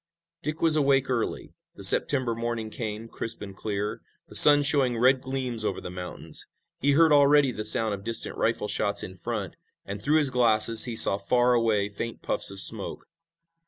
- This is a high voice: No, low, 115 Hz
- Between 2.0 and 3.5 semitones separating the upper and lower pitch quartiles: No, average, 4.3 semitones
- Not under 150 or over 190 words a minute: Yes, average, 185 wpm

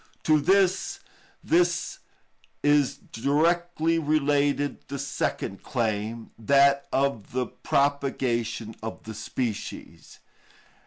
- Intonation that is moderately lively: Yes, average, 4.7 semitones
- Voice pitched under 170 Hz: Yes, medium, 140 Hz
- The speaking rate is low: Yes, slow, 85 wpm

